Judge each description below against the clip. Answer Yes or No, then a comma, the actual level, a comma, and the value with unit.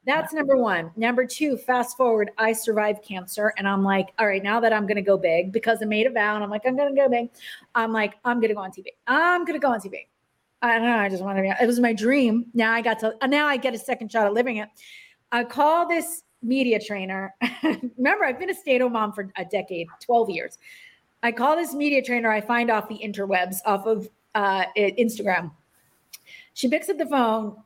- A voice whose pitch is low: No, high, 230 Hz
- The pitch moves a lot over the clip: No, average, 3.6 semitones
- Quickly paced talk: Yes, fast, 230 wpm